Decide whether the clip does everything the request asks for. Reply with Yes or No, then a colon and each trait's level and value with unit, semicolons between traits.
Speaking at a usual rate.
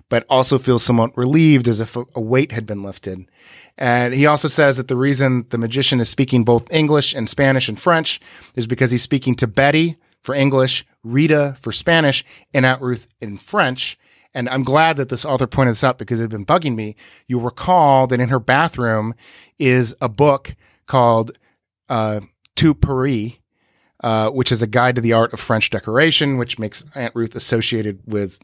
Yes: average, 190 wpm